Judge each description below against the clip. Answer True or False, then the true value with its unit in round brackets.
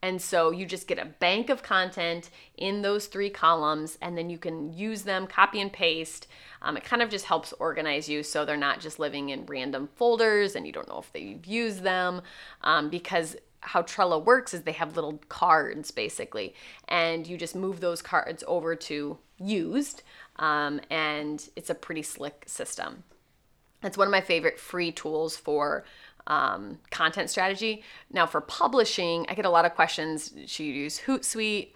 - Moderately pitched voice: True (175 Hz)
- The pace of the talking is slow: False (185 wpm)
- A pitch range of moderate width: True (4.1 semitones)